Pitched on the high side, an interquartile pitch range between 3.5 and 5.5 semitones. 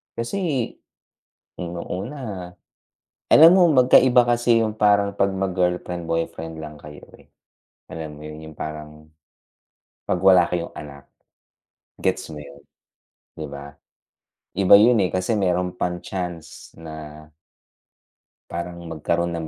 No: very low, 90 Hz; average, 4.4 semitones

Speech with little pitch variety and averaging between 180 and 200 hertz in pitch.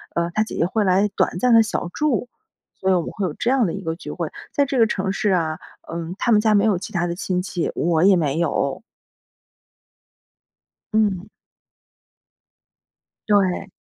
No: average, 3.9 semitones; high, 190 Hz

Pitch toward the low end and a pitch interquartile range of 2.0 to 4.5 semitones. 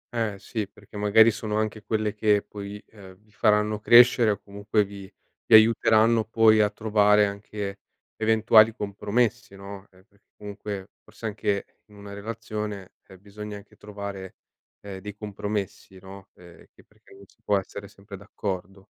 No: low, 105 Hz; narrow, 1.4 semitones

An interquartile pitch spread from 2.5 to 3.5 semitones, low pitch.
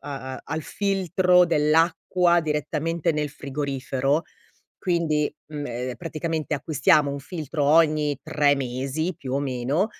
No: average, 2.8 semitones; medium, 150 Hz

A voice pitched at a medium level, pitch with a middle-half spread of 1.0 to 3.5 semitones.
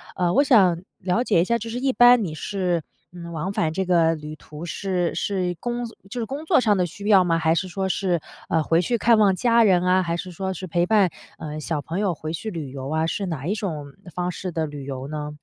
No: medium, 180 Hz; average, 4.0 semitones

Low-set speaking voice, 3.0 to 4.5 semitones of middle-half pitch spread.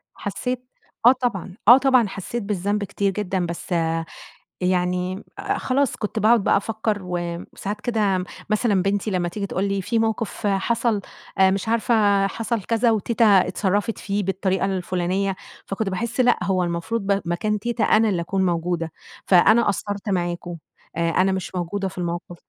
No: high, 195 Hz; average, 3.3 semitones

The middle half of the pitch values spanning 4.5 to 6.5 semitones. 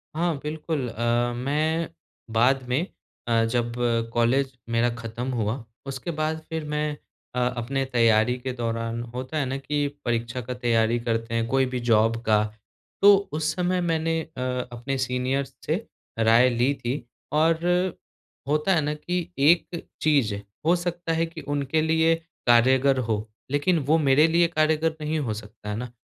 Yes: average, 4.9 semitones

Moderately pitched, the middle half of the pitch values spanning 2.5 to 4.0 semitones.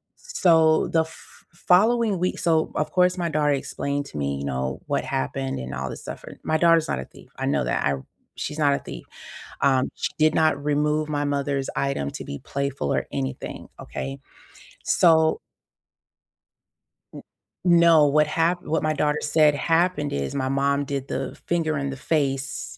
Yes: medium, 150 Hz; average, 2.9 semitones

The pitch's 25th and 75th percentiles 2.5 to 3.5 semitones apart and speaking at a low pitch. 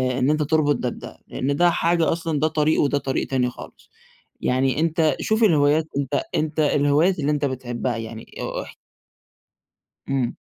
No: average, 3.1 semitones; medium, 145 Hz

